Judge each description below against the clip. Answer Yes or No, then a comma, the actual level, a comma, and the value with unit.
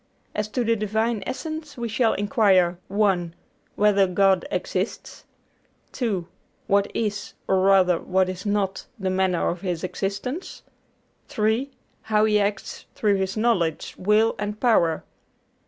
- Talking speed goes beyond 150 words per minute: No, slow, 135 wpm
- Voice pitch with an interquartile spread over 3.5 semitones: No, average, 2.8 semitones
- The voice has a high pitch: Yes, high, 200 Hz